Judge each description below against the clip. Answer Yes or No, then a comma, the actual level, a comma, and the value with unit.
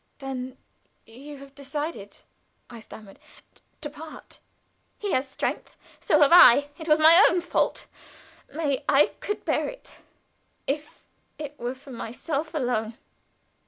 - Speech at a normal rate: No, slow, 130 wpm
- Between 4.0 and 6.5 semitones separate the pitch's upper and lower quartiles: No, average, 3.4 semitones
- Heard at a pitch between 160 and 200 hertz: No, very high, 285 Hz